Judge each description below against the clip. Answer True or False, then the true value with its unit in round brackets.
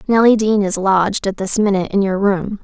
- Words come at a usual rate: False (230 wpm)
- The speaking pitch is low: False (200 Hz)